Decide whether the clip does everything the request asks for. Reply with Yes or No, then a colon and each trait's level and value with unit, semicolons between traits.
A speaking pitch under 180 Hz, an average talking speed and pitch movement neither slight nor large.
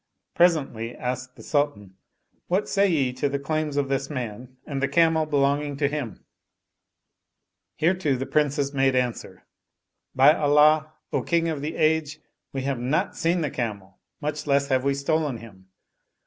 Yes: medium, 140 Hz; average, 165 wpm; average, 3.1 semitones